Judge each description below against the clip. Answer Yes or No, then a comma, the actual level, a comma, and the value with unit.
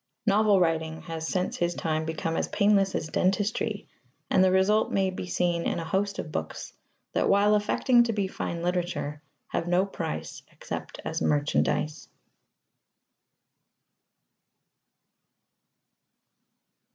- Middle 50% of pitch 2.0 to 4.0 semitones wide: Yes, average, 3.7 semitones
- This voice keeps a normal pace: No, slow, 125 wpm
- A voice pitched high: No, medium, 180 Hz